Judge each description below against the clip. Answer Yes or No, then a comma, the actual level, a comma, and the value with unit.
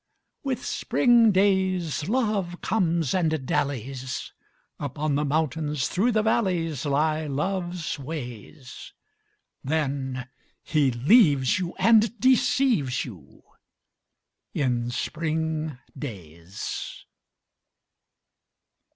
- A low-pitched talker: No, medium, 155 Hz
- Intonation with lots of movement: Yes, wide, 5.7 semitones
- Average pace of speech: No, slow, 80 wpm